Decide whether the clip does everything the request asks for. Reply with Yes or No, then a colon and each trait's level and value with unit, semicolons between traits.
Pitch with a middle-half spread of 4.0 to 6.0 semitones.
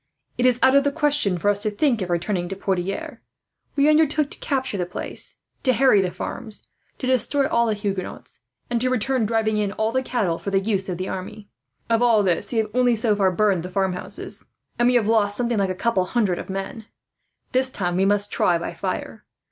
Yes: average, 4.4 semitones